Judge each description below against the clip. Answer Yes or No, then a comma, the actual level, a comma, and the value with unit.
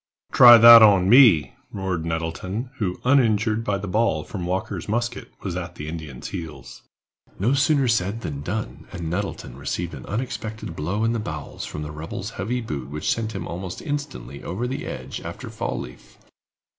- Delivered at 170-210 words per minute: Yes, average, 175 wpm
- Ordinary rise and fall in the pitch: No, wide, 5.9 semitones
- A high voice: No, very low, 95 Hz